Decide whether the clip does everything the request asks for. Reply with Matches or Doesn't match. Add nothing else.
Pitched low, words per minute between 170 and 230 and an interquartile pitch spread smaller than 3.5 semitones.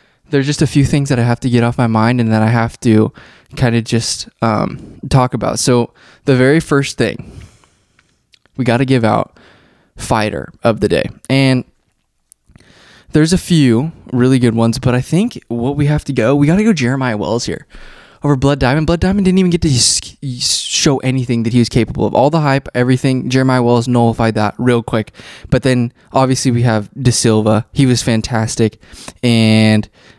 Matches